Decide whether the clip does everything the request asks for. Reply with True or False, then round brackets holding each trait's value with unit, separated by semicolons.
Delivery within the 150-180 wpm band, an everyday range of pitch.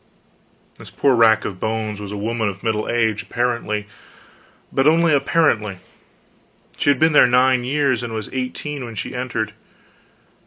True (155 wpm; 3.3 semitones)